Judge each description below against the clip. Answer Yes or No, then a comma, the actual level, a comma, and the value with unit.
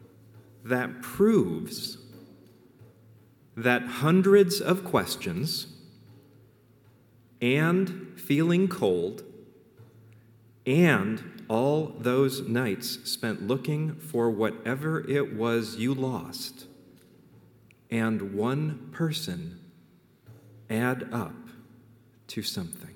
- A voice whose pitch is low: Yes, low, 125 Hz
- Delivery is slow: Yes, slow, 75 wpm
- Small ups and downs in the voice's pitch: No, average, 4.9 semitones